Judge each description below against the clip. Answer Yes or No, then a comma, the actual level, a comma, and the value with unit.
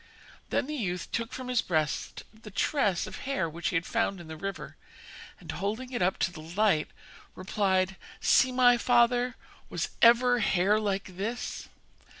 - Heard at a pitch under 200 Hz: No, high, 210 Hz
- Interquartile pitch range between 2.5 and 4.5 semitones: No, average, 5.1 semitones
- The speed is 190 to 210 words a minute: No, average, 165 wpm